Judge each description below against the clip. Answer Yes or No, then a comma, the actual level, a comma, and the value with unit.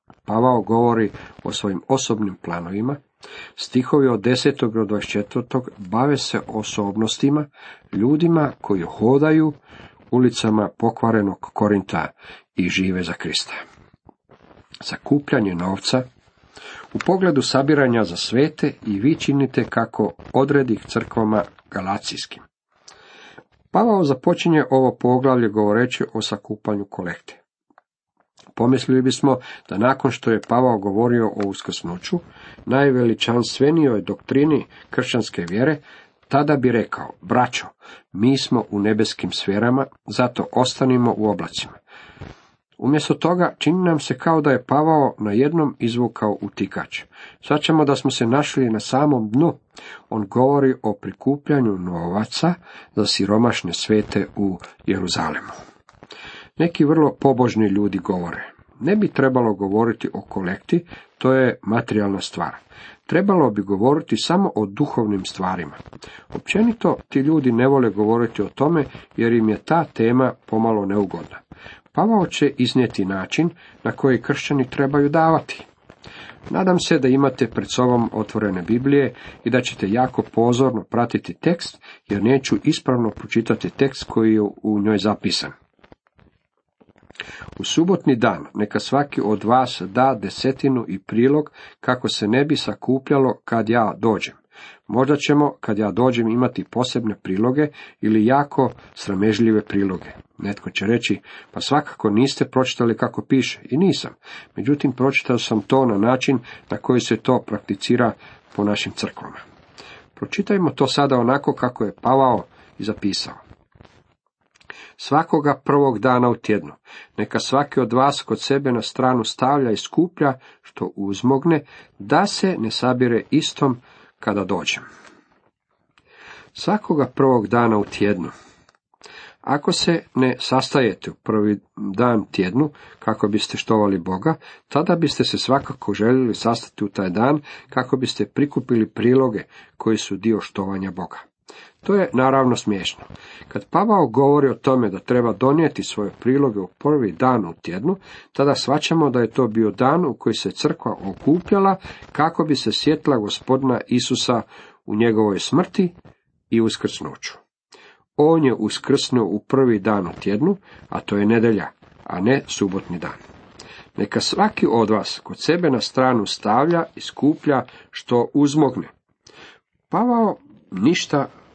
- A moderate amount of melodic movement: Yes, average, 4.7 semitones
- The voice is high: No, low, 125 Hz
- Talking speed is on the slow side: No, average, 130 wpm